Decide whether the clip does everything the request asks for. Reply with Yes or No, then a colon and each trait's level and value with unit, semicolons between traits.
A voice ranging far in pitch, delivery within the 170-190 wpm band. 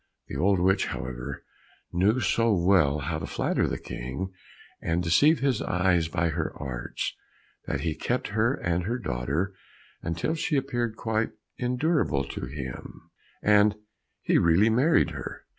No: wide, 6.7 semitones; average, 145 wpm